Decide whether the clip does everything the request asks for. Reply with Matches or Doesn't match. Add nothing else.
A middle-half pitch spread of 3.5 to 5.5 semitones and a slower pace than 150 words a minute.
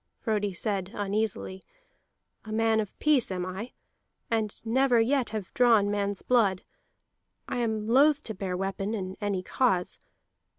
Doesn't match